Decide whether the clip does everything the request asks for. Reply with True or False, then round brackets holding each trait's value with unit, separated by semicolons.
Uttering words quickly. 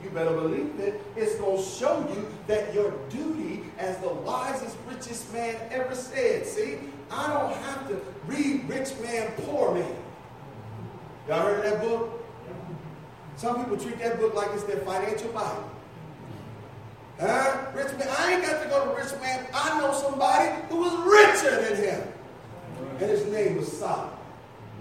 False (165 wpm)